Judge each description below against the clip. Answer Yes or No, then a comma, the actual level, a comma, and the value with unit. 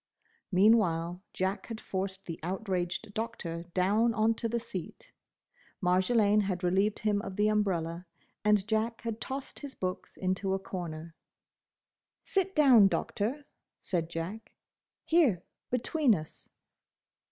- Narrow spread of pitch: No, average, 3.8 semitones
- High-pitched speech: Yes, high, 200 Hz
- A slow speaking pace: Yes, slow, 125 wpm